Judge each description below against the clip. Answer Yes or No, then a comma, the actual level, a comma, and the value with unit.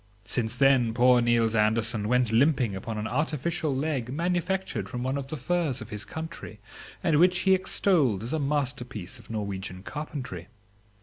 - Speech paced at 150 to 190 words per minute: Yes, average, 165 wpm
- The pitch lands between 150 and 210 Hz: No, low, 125 Hz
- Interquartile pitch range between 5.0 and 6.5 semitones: Yes, wide, 5.6 semitones